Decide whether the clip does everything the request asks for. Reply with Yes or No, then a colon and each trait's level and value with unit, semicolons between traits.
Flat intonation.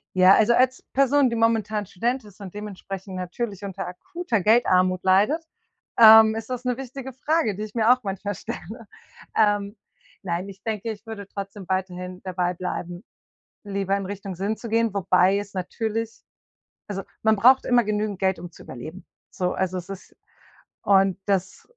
No: average, 3.2 semitones